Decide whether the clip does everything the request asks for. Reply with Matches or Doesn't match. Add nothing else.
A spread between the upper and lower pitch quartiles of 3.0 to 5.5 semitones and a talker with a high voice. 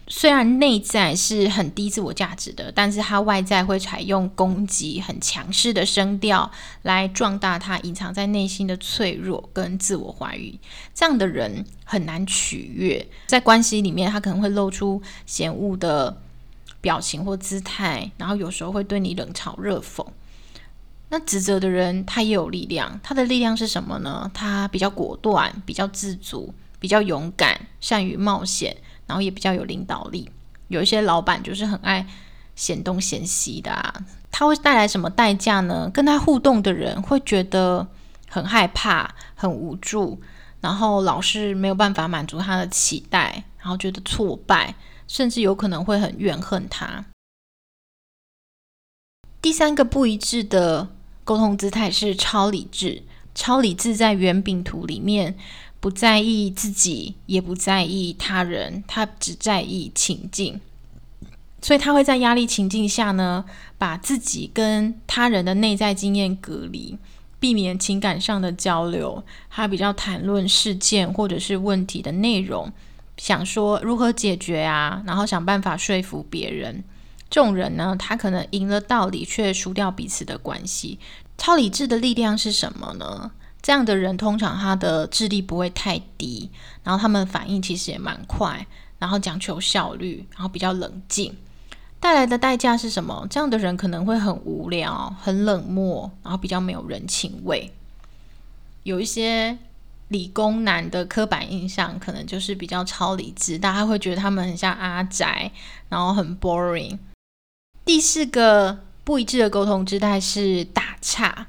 Doesn't match